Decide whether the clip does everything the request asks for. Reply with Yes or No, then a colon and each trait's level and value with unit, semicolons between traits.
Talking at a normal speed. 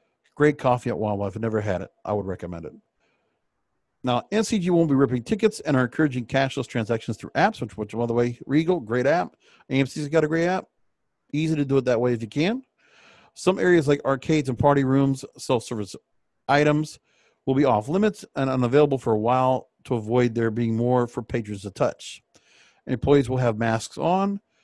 Yes: average, 195 wpm